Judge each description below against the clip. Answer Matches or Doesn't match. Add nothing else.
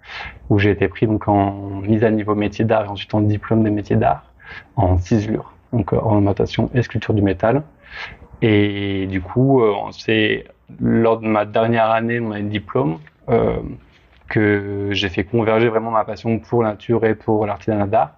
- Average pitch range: Doesn't match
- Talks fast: Doesn't match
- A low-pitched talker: Matches